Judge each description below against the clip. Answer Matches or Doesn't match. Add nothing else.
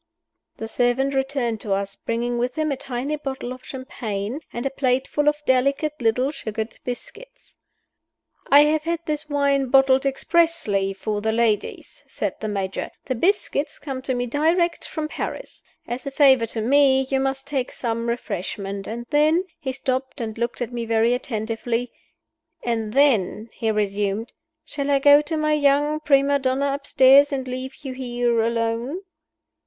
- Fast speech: Doesn't match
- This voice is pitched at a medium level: Doesn't match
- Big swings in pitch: Doesn't match